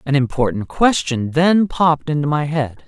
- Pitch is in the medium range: Yes, medium, 150 Hz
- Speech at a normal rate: Yes, average, 165 wpm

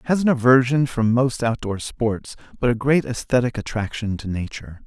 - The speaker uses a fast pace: No, average, 175 wpm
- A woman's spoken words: No, male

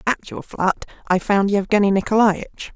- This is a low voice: No, high, 200 Hz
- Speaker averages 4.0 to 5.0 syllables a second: Yes, 4.6 syllables/s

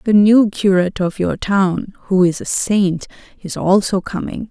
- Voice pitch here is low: No, high, 195 Hz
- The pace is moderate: Yes, average, 175 wpm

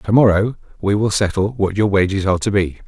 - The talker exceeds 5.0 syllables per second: Yes, 5.9 syllables/s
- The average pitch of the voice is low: Yes, low, 100 Hz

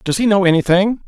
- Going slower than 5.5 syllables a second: No, 5.9 syllables/s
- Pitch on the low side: No, high, 195 Hz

